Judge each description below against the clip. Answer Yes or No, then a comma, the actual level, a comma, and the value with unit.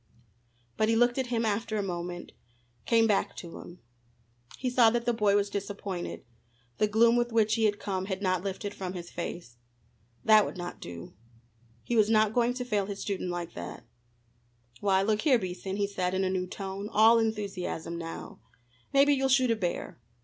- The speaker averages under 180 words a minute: No, average, 190 wpm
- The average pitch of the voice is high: Yes, high, 205 Hz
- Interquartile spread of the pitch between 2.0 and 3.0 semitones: No, average, 3.5 semitones